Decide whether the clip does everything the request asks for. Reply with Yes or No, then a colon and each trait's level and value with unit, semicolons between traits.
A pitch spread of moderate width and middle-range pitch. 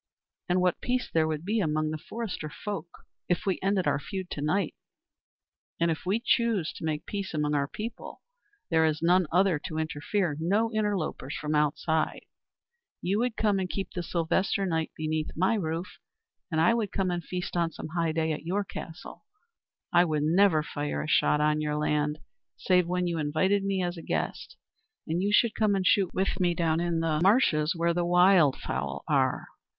Yes: average, 3.8 semitones; medium, 170 Hz